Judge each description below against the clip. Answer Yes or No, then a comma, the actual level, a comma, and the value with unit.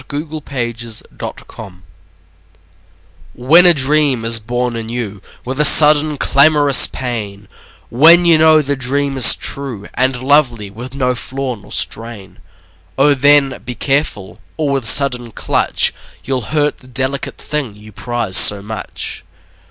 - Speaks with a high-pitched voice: No, low, 130 Hz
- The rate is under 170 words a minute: Yes, average, 150 wpm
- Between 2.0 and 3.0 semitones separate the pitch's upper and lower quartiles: No, average, 3.8 semitones